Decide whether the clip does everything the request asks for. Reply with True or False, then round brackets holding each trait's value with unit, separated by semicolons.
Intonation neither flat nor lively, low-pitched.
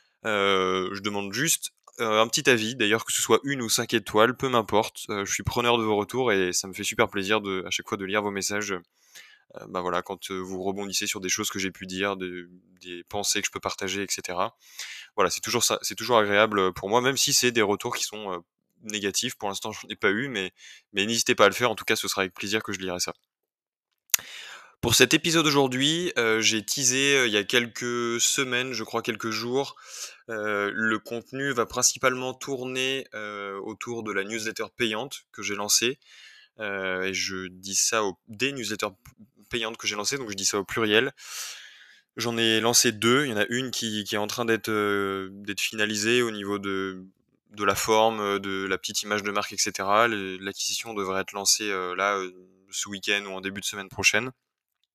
True (3.2 semitones; 105 Hz)